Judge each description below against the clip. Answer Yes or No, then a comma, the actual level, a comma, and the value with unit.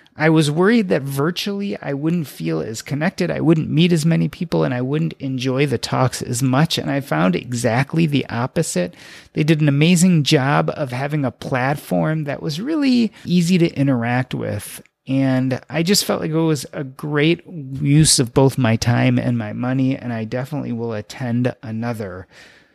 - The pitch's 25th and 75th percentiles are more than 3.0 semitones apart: Yes, average, 4.5 semitones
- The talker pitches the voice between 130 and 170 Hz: Yes, medium, 140 Hz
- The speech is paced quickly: No, average, 180 wpm